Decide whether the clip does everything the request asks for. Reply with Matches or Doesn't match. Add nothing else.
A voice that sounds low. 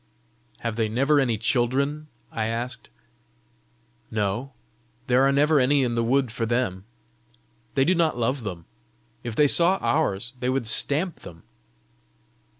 Matches